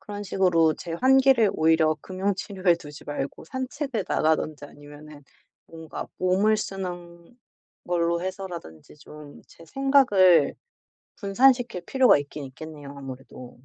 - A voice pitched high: No, medium, 175 Hz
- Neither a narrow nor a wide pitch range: Yes, average, 5.0 semitones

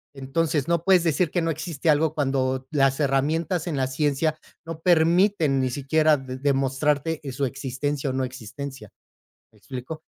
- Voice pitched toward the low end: No, medium, 145 Hz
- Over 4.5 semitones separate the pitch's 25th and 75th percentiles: No, average, 3.2 semitones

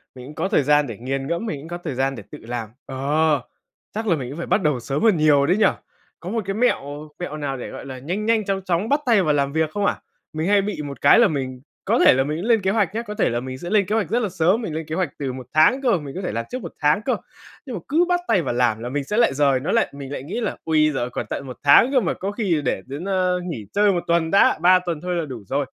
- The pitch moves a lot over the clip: Yes, wide, 6.2 semitones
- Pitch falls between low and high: Yes, medium, 160 Hz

